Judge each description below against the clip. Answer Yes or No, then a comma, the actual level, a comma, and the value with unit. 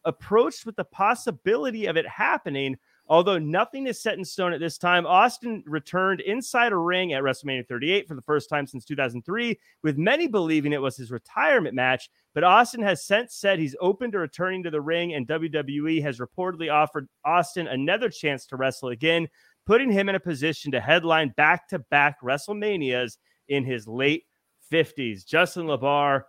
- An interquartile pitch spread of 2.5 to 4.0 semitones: No, average, 5.2 semitones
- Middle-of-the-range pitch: Yes, medium, 160 Hz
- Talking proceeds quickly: No, average, 175 wpm